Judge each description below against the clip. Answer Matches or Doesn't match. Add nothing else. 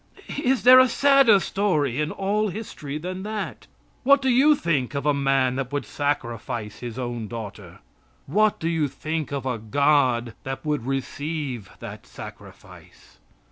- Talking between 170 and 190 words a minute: Doesn't match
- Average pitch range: Doesn't match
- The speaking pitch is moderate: Matches